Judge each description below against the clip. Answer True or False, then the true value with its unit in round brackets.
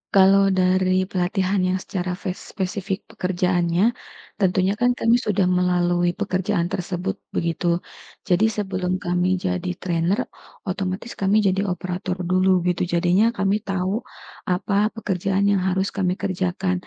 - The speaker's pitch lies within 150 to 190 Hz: True (185 Hz)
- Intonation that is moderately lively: False (1.6 semitones)